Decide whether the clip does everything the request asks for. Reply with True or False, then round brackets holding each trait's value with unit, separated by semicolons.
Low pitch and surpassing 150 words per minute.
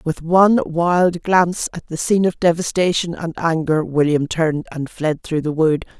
False (165 Hz; 180 wpm)